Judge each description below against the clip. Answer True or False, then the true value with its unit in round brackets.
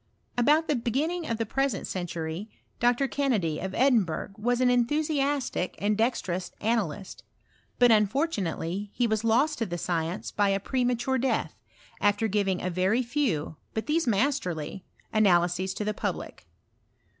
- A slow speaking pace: False (150 wpm)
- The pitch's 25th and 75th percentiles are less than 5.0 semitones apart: False (5.5 semitones)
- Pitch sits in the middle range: False (220 Hz)